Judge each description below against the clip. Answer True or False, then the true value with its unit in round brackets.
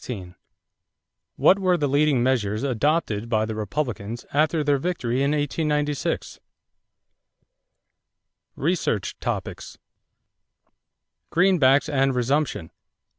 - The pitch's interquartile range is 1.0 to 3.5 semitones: False (4.3 semitones)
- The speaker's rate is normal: False (85 wpm)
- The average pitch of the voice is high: False (140 Hz)